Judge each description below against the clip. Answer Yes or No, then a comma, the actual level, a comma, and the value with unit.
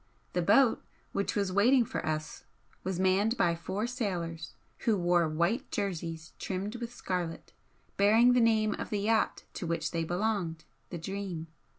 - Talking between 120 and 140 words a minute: No, average, 160 wpm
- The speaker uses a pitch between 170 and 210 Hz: Yes, high, 190 Hz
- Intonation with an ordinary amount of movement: Yes, average, 4.3 semitones